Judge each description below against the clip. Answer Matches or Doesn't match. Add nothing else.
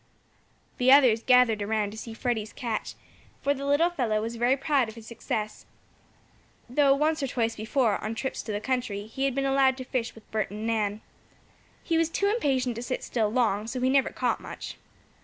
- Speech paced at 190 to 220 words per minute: Matches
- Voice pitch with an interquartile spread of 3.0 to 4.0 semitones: Matches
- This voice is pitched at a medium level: Doesn't match